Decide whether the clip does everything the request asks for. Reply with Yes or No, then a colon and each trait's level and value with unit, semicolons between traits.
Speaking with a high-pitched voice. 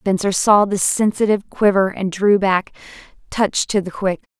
Yes: high, 195 Hz